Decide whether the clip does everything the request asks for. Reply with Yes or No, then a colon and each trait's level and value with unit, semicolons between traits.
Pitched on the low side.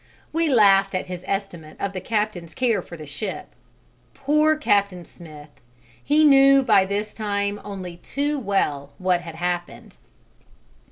No: high, 195 Hz